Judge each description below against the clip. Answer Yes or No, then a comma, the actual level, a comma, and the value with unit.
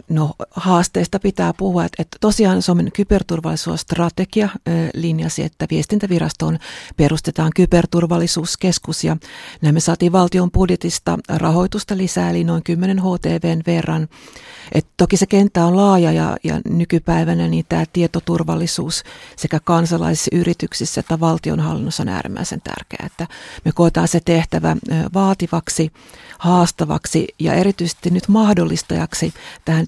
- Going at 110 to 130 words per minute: Yes, average, 120 wpm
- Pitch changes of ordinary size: No, narrow, 2.1 semitones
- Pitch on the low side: No, medium, 170 Hz